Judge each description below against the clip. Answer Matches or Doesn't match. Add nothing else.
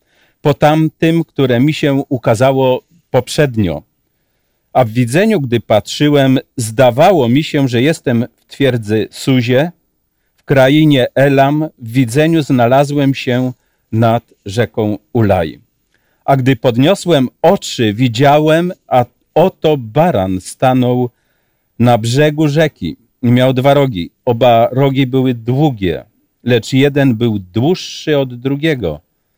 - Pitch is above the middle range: Doesn't match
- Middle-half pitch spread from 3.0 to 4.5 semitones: Matches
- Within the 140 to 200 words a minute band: Doesn't match